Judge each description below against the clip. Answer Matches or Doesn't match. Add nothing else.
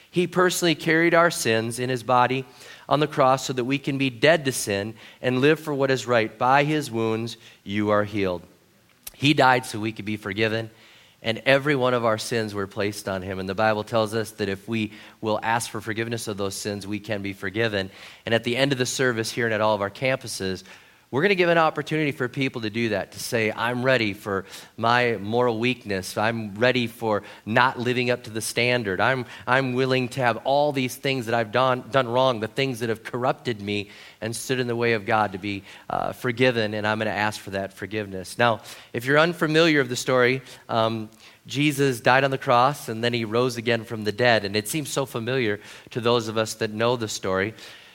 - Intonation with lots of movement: Doesn't match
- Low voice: Matches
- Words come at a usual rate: Doesn't match